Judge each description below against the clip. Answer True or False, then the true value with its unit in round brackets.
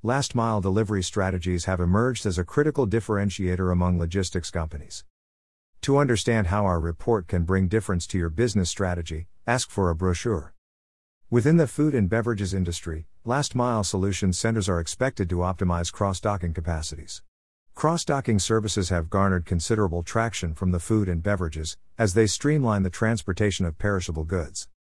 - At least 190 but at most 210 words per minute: False (155 wpm)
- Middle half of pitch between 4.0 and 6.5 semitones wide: True (4.4 semitones)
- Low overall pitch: True (95 Hz)